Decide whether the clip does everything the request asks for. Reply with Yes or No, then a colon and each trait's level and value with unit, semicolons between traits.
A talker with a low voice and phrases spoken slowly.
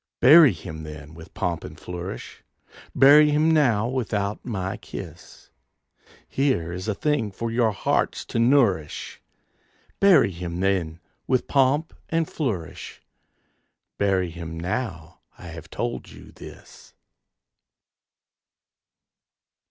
Yes: low, 100 Hz; slow, 115 wpm